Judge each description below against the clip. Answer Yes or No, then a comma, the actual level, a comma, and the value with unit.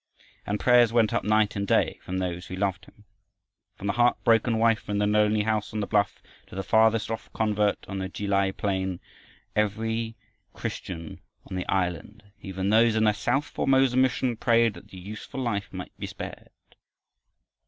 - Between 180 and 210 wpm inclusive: Yes, average, 185 wpm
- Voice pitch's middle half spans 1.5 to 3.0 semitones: Yes, narrow, 2.6 semitones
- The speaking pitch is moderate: No, low, 105 Hz